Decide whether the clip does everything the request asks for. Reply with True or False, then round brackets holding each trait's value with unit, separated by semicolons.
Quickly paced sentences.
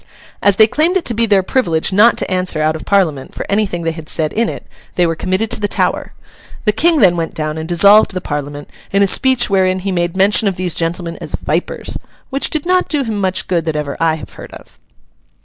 True (235 wpm)